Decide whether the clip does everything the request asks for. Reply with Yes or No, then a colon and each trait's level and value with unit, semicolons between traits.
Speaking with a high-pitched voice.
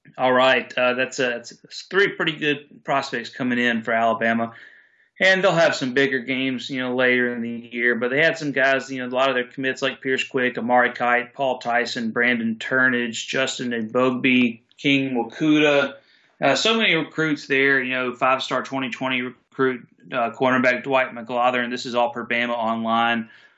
No: low, 125 Hz